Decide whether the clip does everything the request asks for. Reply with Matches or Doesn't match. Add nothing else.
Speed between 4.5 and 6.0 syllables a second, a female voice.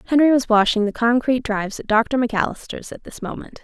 Doesn't match